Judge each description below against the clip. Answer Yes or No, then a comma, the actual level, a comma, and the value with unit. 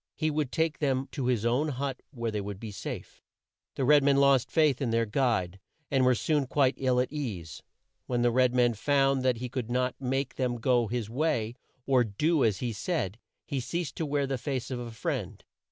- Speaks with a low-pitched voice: Yes, low, 130 Hz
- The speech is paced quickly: Yes, fast, 215 wpm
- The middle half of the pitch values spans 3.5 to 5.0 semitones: No, average, 3.0 semitones